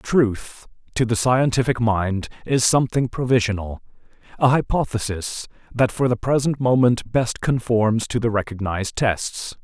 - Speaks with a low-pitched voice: Yes, low, 115 Hz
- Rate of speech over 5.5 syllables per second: No, 4.4 syllables/s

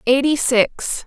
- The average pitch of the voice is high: Yes, very high, 265 Hz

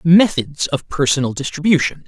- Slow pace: Yes, slow, 115 wpm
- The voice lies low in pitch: No, medium, 150 Hz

